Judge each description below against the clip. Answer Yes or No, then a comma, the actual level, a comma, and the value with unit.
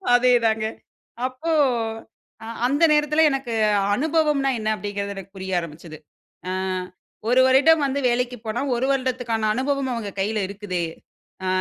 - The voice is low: No, high, 245 Hz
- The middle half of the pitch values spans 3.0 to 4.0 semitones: No, average, 4.8 semitones